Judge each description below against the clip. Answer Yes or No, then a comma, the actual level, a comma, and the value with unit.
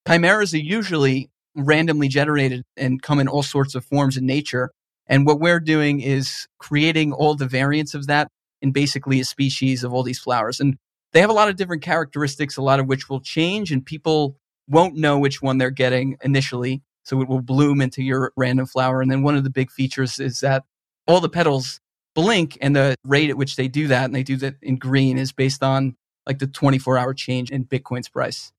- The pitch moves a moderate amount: No, narrow, 2.1 semitones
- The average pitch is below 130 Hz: No, low, 135 Hz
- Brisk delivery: Yes, fast, 215 wpm